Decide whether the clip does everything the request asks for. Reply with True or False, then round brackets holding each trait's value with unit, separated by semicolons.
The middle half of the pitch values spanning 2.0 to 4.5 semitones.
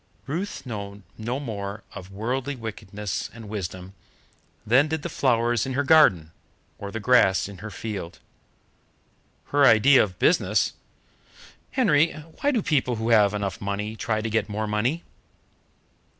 False (5.2 semitones)